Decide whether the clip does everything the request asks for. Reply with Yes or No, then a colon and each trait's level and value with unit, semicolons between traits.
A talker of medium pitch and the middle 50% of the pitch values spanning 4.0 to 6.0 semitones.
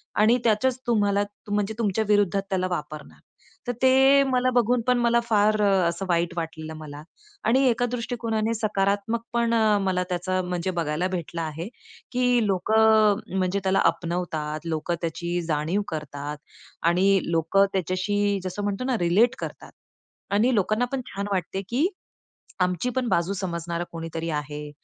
No: high, 195 Hz; average, 4.7 semitones